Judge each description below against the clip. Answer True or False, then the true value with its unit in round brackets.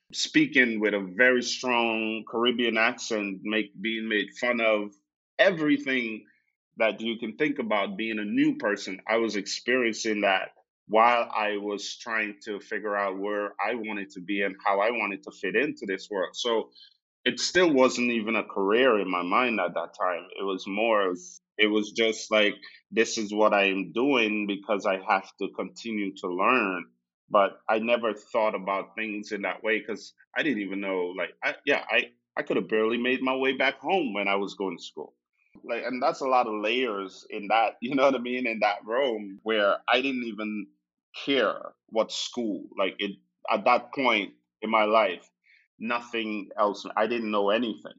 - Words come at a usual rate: True (190 wpm)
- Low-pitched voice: True (110 Hz)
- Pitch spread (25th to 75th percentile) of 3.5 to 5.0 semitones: False (3.0 semitones)